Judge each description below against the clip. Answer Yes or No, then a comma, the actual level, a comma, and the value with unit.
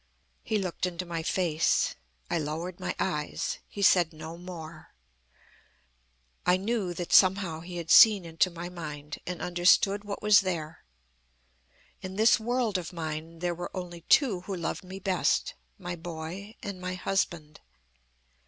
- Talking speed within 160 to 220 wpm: No, average, 150 wpm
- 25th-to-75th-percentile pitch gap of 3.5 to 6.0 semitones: No, narrow, 2.5 semitones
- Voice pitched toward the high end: No, medium, 180 Hz